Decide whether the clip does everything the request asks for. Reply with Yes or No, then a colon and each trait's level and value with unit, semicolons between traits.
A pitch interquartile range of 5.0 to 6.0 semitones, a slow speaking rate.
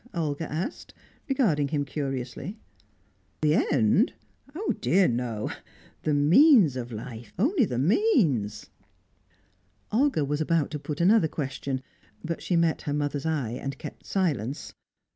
Yes: average, 5.3 semitones; slow, 130 wpm